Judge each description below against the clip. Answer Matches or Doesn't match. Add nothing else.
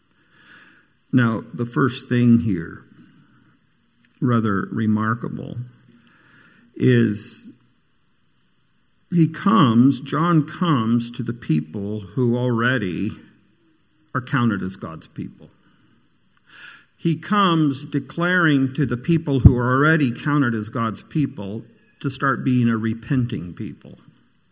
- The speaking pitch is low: Matches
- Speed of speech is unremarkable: Doesn't match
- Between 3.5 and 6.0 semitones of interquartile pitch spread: Matches